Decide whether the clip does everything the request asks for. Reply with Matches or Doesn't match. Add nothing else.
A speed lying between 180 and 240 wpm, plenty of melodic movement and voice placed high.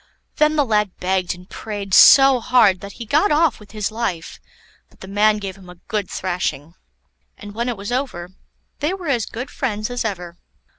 Doesn't match